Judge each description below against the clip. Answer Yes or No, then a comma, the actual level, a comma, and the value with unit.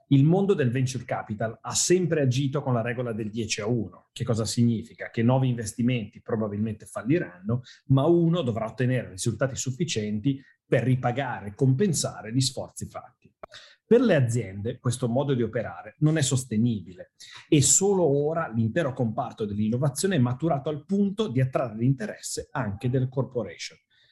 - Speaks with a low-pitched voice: Yes, low, 125 Hz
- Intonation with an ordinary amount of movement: Yes, average, 3.7 semitones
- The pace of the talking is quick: No, average, 155 wpm